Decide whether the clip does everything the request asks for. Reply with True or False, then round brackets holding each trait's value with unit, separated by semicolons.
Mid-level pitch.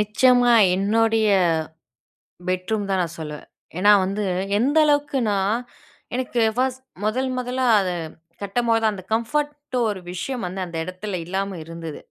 False (215 Hz)